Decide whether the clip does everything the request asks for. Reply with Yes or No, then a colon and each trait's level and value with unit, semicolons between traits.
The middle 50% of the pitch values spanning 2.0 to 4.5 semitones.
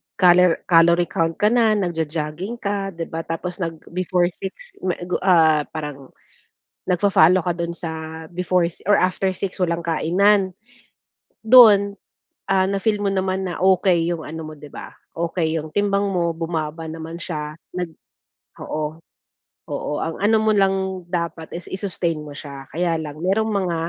Yes: average, 2.9 semitones